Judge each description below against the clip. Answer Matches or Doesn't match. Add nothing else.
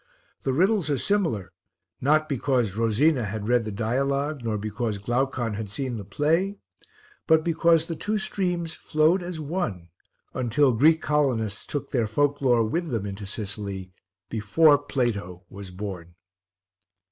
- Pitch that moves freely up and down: Matches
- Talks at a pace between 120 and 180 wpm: Matches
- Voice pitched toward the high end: Doesn't match